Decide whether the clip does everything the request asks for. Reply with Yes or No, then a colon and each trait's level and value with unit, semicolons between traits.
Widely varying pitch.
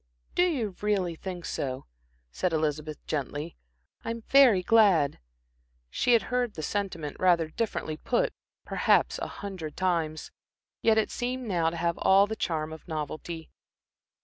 Yes: wide, 5.7 semitones